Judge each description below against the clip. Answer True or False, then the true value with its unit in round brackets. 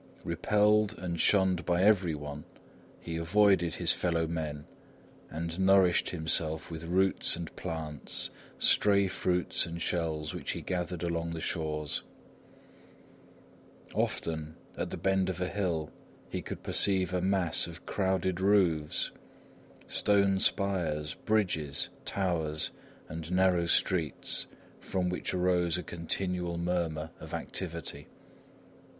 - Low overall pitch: True (85 Hz)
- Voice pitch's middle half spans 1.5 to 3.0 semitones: True (2.7 semitones)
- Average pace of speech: False (120 wpm)